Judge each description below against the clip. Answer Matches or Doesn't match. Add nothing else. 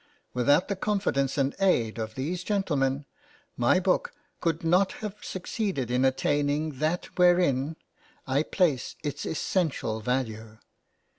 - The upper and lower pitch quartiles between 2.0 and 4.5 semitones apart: Doesn't match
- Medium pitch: Matches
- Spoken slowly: Matches